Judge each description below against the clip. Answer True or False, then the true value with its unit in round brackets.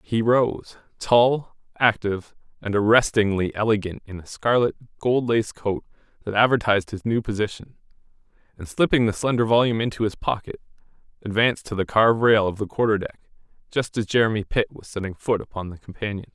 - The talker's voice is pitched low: True (110 Hz)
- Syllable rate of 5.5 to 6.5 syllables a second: True (5.8 syllables/s)